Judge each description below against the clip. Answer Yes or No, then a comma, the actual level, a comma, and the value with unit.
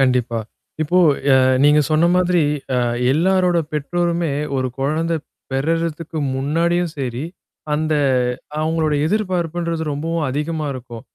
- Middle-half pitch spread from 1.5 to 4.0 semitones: Yes, average, 3.0 semitones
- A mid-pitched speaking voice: Yes, medium, 160 Hz